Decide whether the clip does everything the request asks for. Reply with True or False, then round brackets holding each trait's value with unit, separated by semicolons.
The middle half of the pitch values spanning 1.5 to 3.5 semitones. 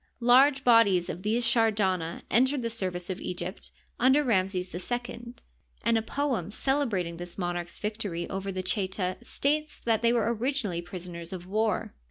False (4.7 semitones)